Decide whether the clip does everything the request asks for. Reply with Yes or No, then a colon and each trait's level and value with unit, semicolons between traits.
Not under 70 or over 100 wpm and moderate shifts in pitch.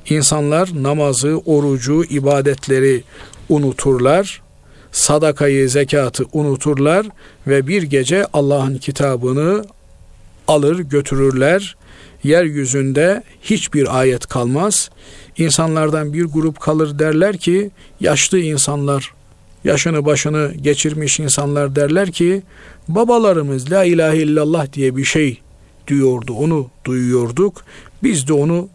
Yes: slow, 95 wpm; average, 3.1 semitones